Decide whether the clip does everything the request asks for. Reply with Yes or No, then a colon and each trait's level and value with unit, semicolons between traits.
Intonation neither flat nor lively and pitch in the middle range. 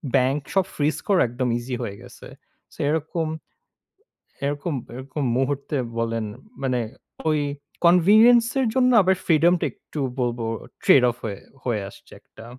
No: wide, 5.9 semitones; medium, 145 Hz